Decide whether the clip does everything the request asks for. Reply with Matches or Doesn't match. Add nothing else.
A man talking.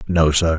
Matches